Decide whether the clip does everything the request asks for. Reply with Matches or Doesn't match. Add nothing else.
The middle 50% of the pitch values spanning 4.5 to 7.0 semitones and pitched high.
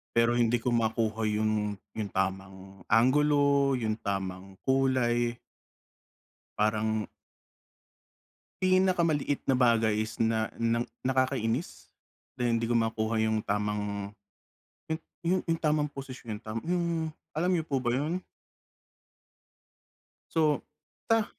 Doesn't match